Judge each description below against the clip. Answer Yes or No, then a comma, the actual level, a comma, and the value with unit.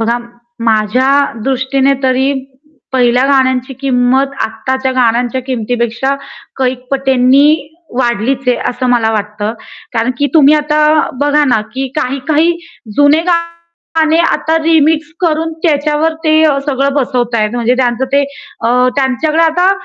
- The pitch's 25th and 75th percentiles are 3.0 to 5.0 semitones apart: Yes, average, 3.5 semitones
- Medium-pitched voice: No, very high, 265 Hz